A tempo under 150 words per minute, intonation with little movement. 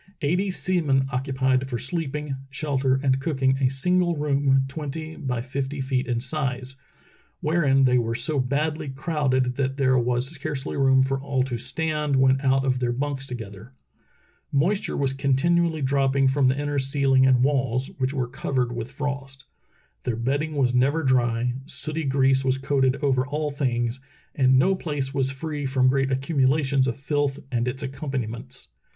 No: average, 165 wpm; narrow, 1.9 semitones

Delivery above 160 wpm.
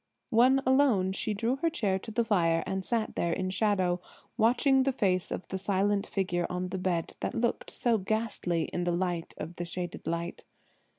Yes: average, 190 wpm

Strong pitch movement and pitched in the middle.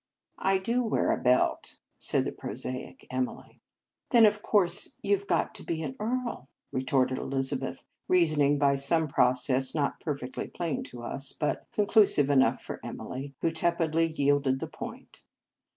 No: average, 4.8 semitones; medium, 145 Hz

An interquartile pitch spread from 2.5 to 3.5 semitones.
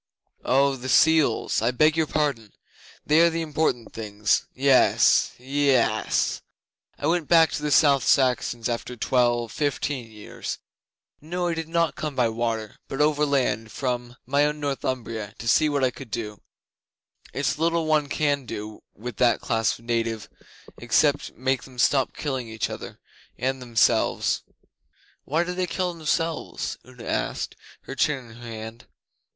No: average, 4.4 semitones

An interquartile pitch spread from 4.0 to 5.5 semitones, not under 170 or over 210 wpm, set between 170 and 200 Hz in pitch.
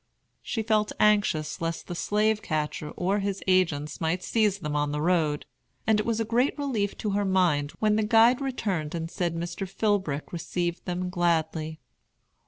Yes: average, 4.6 semitones; average, 175 wpm; medium, 185 Hz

